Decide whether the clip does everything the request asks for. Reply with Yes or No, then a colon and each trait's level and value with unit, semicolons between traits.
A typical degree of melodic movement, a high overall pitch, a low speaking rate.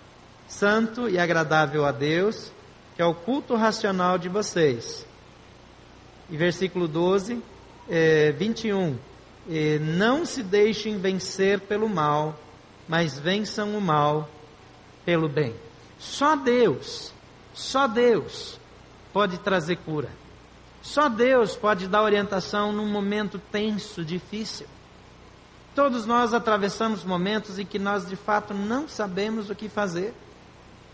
Yes: average, 4.7 semitones; high, 200 Hz; slow, 115 wpm